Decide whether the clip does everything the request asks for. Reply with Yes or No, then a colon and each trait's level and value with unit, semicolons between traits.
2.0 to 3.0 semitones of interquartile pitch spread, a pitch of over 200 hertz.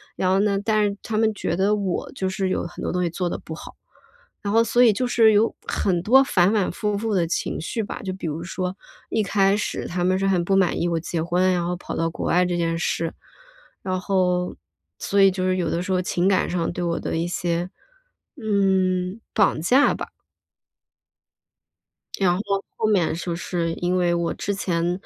No: narrow, 2.5 semitones; medium, 185 Hz